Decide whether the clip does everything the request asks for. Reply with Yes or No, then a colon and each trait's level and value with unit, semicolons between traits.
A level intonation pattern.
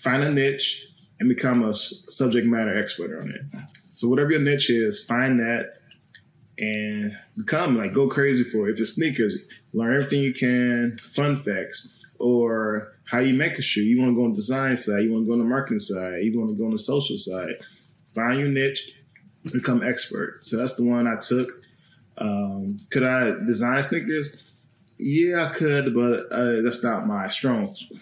No: average, 3.3 semitones